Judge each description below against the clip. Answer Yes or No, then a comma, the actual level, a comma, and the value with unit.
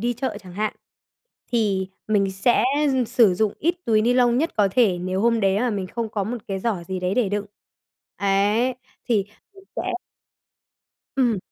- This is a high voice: Yes, high, 215 Hz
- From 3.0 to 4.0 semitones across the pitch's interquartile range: Yes, average, 3.7 semitones